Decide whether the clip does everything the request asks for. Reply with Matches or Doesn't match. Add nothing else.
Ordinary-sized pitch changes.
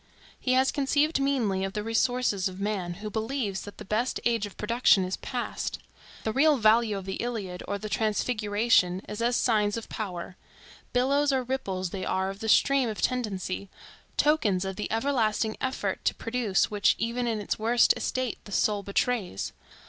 Matches